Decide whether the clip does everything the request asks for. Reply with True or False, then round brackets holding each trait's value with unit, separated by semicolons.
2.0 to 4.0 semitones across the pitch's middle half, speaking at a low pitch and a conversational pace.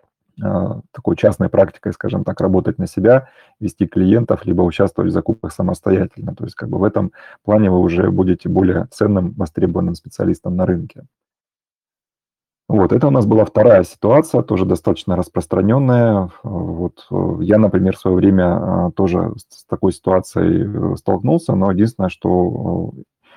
True (2.9 semitones; 95 Hz; 140 wpm)